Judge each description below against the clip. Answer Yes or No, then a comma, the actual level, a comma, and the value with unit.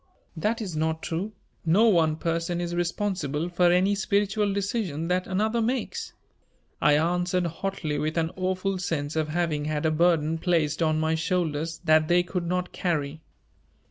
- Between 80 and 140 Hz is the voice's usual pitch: No, medium, 175 Hz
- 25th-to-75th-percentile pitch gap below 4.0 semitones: Yes, average, 2.8 semitones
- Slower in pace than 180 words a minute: Yes, average, 160 wpm